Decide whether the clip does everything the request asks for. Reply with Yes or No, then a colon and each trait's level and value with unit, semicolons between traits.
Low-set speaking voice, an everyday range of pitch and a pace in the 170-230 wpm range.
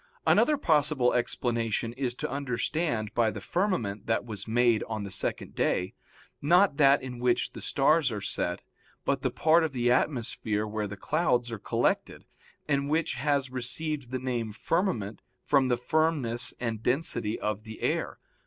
No: low, 125 Hz; average, 4.4 semitones; average, 160 wpm